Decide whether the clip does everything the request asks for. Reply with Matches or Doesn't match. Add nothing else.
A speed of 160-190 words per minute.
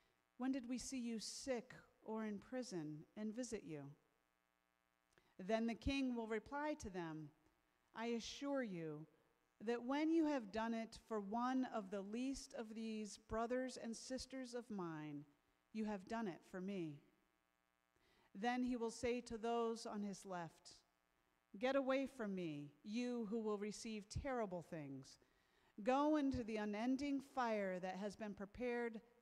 Doesn't match